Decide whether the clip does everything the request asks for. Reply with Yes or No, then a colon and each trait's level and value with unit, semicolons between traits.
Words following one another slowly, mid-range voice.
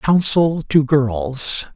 Yes: slow, 105 wpm; medium, 145 Hz